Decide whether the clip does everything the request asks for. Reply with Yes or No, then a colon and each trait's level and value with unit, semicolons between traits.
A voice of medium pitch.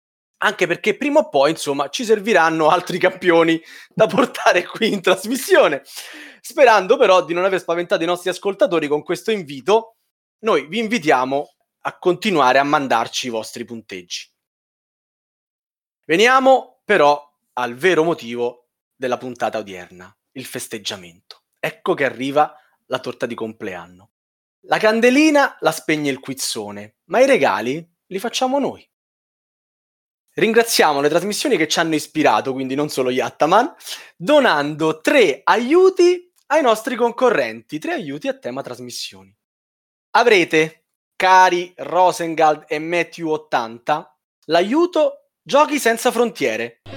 Yes: medium, 165 Hz